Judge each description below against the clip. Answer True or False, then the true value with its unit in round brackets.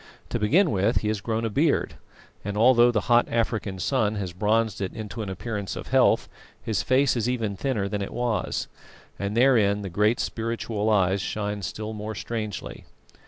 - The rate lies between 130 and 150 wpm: False (180 wpm)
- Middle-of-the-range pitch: False (110 Hz)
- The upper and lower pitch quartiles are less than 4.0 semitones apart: True (2.5 semitones)